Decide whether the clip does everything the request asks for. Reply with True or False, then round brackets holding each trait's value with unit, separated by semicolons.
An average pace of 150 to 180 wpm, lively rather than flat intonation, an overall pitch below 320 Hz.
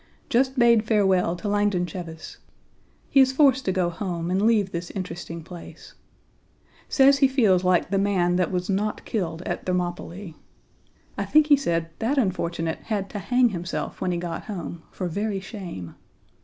False (170 wpm; 3.9 semitones; 190 Hz)